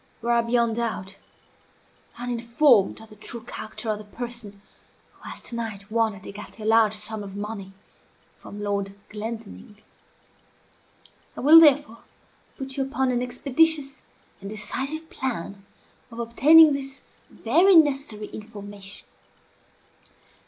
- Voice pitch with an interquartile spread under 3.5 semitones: No, average, 4.2 semitones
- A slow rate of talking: Yes, slow, 130 wpm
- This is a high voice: Yes, high, 230 Hz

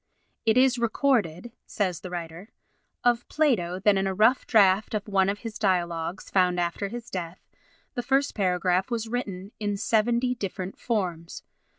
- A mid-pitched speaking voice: No, high, 200 Hz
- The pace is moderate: Yes, average, 160 wpm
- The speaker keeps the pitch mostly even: No, average, 4.5 semitones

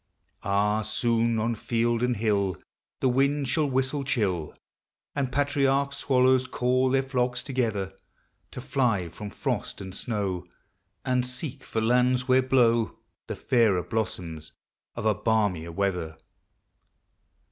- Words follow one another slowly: Yes, slow, 125 wpm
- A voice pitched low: Yes, low, 120 Hz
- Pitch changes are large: No, average, 4.2 semitones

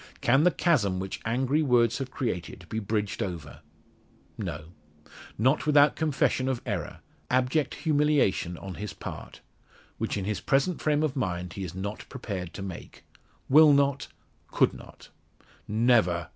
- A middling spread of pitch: No, wide, 6.9 semitones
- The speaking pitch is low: Yes, low, 120 Hz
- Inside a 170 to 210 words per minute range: No, average, 145 wpm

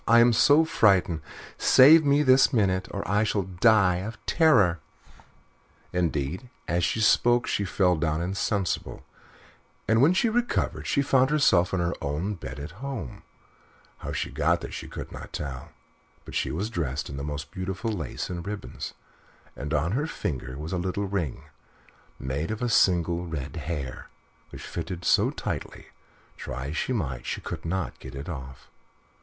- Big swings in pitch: Yes, wide, 6.5 semitones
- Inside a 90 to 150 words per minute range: No, average, 170 wpm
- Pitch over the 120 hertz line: No, very low, 90 Hz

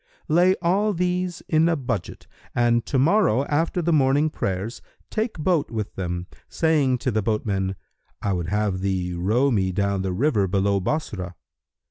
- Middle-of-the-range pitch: No, low, 120 Hz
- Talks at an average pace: Yes, average, 160 wpm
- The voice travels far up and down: Yes, wide, 8.5 semitones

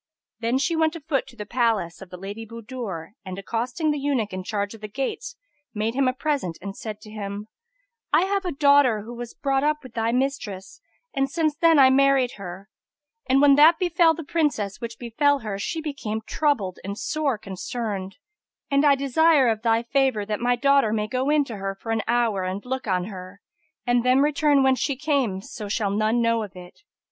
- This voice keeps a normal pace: No, fast, 210 wpm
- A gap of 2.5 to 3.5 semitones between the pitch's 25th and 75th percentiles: No, average, 5.1 semitones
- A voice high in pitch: Yes, high, 240 Hz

